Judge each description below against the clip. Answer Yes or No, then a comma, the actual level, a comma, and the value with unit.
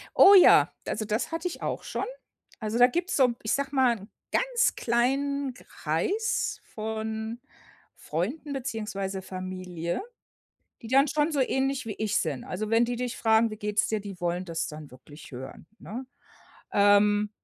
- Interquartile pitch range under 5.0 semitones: No, average, 5.3 semitones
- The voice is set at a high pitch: Yes, high, 220 Hz